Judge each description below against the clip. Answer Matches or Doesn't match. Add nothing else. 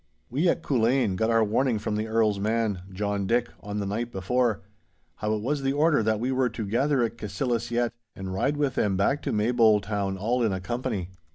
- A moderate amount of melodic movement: Matches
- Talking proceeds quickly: Matches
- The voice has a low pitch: Matches